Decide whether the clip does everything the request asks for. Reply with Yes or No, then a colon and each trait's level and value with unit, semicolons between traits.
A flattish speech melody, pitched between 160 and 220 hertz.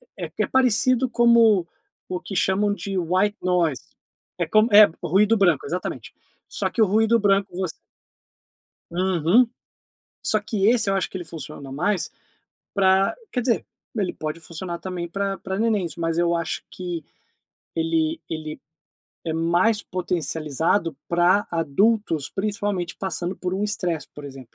No: average, 3.8 semitones; high, 190 Hz